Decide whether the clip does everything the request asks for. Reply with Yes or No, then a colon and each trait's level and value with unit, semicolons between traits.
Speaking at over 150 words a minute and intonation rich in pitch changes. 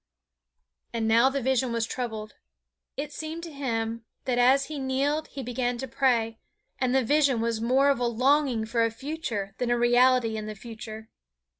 No: average, 180 wpm; average, 3.0 semitones